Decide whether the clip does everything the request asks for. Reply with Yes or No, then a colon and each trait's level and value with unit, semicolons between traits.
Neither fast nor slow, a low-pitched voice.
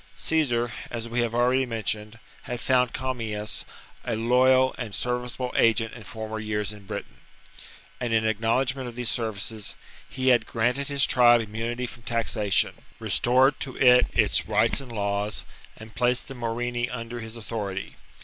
Yes: average, 160 wpm; low, 120 Hz